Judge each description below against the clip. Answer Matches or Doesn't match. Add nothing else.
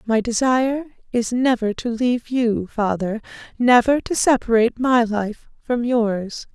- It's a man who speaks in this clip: Doesn't match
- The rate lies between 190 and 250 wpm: Doesn't match